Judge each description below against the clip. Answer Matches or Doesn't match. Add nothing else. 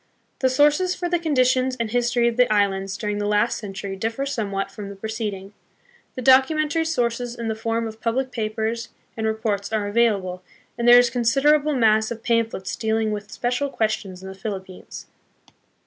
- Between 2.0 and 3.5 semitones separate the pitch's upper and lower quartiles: Matches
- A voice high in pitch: Matches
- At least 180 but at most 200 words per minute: Matches